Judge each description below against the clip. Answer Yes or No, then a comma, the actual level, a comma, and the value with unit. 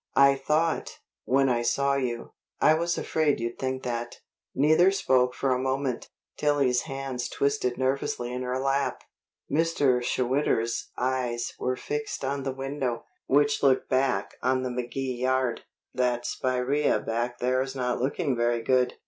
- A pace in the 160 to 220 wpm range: No, average, 150 wpm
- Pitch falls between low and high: No, low, 130 Hz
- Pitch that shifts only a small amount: Yes, narrow, 1.9 semitones